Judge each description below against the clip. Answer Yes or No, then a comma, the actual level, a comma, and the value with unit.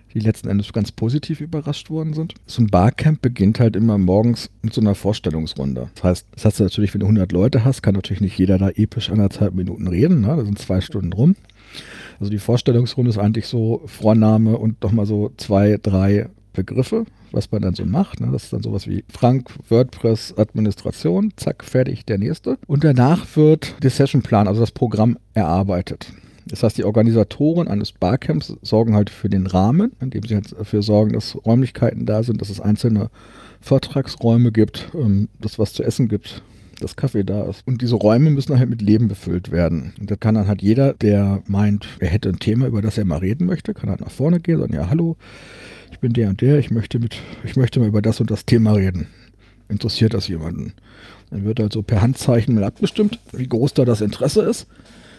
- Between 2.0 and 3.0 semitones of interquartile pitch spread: No, average, 3.6 semitones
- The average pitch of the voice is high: No, low, 110 Hz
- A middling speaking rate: No, fast, 205 wpm